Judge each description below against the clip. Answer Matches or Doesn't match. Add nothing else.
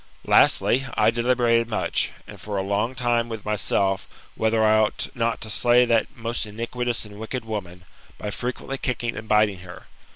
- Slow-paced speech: Doesn't match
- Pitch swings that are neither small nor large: Doesn't match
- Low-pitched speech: Matches